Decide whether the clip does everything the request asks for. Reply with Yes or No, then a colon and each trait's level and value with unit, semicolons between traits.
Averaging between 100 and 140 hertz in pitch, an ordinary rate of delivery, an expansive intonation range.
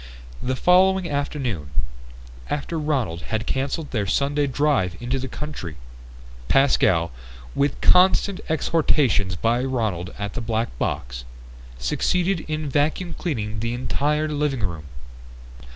No: low, 135 Hz; slow, 120 wpm; wide, 6.1 semitones